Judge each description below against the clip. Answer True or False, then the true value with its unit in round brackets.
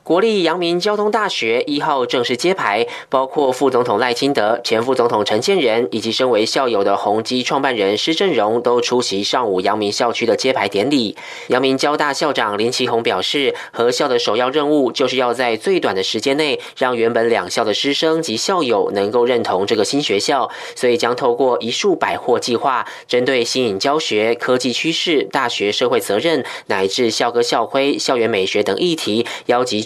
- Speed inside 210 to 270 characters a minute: False (295 characters per minute)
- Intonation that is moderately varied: False (5.7 semitones)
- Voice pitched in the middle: False (125 Hz)